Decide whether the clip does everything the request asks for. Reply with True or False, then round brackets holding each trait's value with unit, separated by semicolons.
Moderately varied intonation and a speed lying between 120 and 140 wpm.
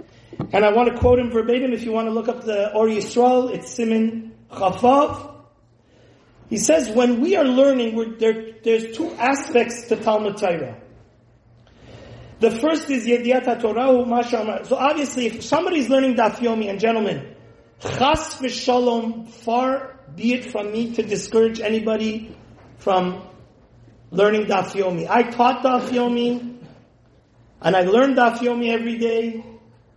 True (3.1 semitones; 135 wpm)